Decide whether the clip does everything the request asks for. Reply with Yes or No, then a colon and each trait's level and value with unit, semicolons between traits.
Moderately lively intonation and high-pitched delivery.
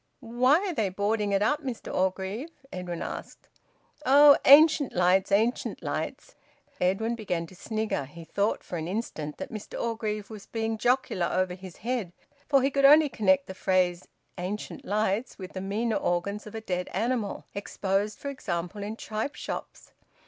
Yes: average, 4.3 semitones; high, 210 Hz